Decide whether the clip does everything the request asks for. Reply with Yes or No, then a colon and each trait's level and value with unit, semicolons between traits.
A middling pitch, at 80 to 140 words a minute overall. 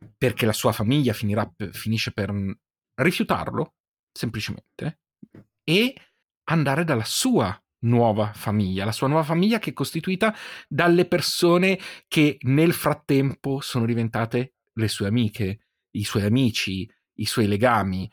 No: low, 120 Hz; average, 125 wpm